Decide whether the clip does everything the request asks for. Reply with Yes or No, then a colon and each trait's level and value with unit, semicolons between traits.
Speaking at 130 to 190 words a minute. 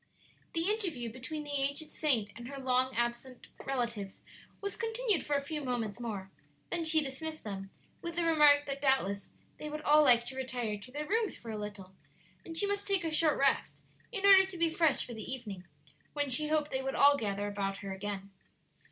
No: fast, 205 wpm